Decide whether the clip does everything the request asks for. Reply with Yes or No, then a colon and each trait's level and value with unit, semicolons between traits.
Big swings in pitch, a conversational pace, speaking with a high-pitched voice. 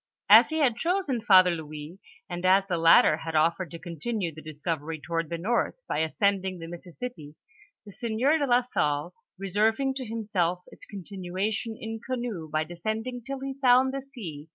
Yes: wide, 6.4 semitones; average, 180 wpm; high, 195 Hz